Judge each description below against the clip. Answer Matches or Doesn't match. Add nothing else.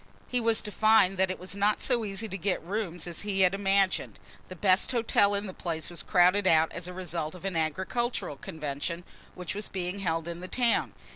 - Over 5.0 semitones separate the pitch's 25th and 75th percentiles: Doesn't match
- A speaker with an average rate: Doesn't match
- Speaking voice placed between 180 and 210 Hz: Matches